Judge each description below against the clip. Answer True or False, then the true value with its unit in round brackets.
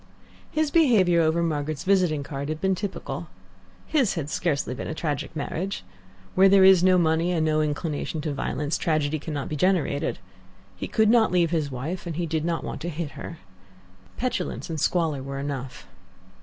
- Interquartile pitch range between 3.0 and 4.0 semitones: True (3.7 semitones)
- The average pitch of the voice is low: False (160 Hz)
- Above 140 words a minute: True (180 wpm)